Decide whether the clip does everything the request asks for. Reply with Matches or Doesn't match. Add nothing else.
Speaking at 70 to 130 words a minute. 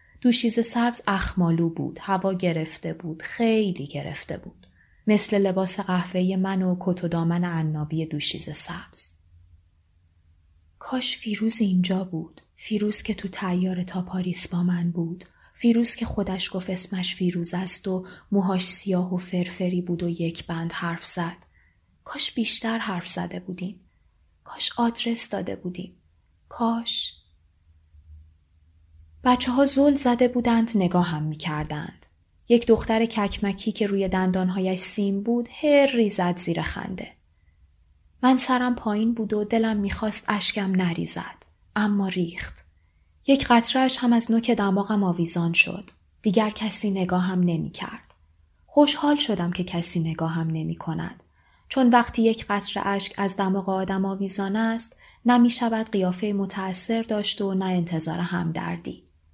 Doesn't match